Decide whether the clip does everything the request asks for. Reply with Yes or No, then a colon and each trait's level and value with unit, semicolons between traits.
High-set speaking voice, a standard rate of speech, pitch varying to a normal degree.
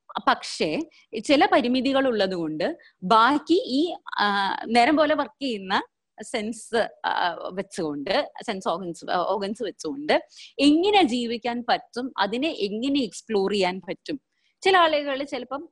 No: very high, 255 Hz; average, 105 wpm; wide, 6.9 semitones